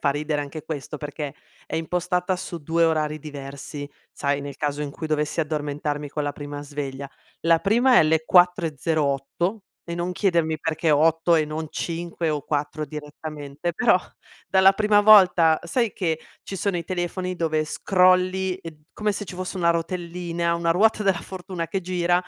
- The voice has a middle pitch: Yes, medium, 165 Hz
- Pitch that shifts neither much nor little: Yes, average, 3.3 semitones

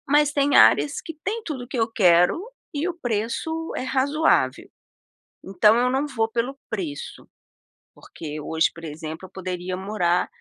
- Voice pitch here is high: Yes, high, 225 Hz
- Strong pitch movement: Yes, wide, 7.9 semitones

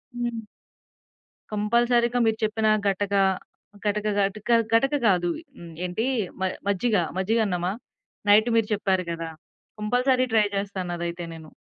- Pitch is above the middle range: Yes, high, 210 Hz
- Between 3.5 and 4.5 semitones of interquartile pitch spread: Yes, average, 3.8 semitones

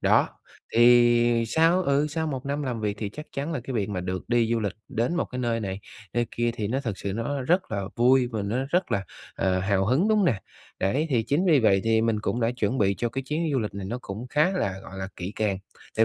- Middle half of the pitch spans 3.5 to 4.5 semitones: No, average, 5.1 semitones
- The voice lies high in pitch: No, low, 120 Hz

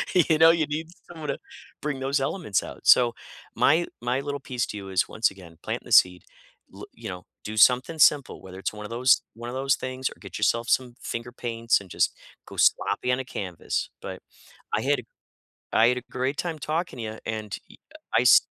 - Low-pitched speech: Yes, low, 125 Hz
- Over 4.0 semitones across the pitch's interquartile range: Yes, average, 4.5 semitones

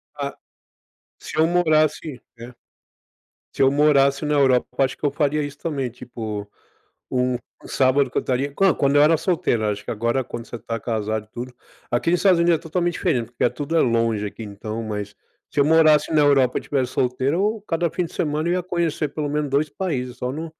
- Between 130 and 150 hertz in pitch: Yes, medium, 140 Hz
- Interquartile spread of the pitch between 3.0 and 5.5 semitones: Yes, average, 4.3 semitones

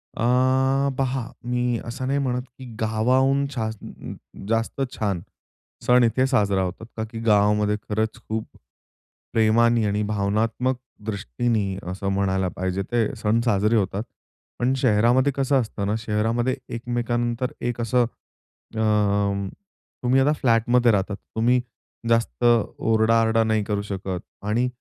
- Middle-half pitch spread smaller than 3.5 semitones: Yes, average, 2.8 semitones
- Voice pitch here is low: Yes, low, 115 Hz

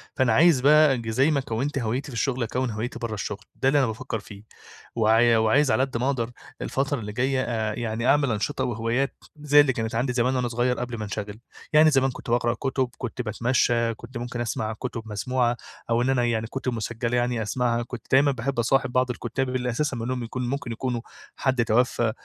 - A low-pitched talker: Yes, low, 120 Hz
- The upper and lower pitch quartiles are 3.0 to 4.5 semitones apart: No, narrow, 2.4 semitones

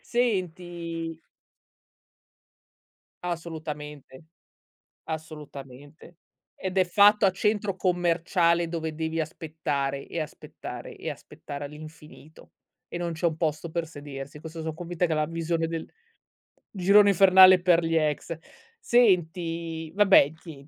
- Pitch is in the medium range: Yes, medium, 165 Hz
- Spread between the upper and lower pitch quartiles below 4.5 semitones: Yes, narrow, 2.4 semitones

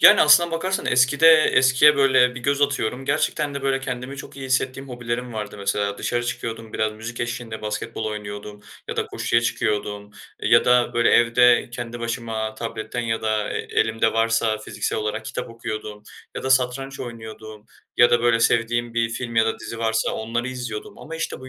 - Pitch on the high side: No, low, 120 Hz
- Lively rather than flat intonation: No, narrow, 2.6 semitones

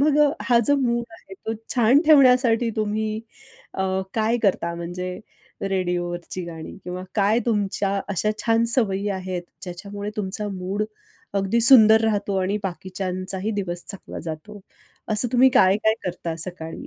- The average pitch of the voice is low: No, high, 200 Hz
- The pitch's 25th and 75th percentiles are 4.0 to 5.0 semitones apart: No, average, 3.3 semitones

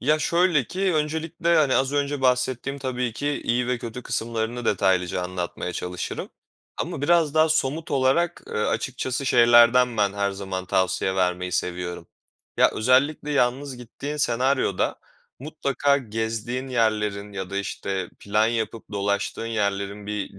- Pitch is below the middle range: Yes, low, 120 Hz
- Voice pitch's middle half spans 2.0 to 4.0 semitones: No, wide, 5.6 semitones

